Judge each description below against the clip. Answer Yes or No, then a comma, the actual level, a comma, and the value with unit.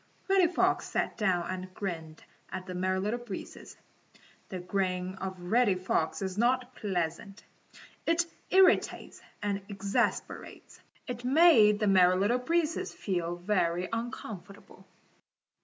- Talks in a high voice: Yes, high, 195 Hz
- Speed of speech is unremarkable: No, slow, 125 wpm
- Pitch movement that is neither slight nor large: Yes, average, 4.8 semitones